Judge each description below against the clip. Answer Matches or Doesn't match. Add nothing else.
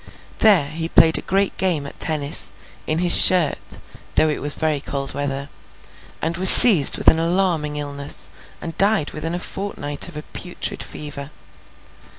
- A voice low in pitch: Doesn't match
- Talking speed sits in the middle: Matches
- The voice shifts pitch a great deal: Doesn't match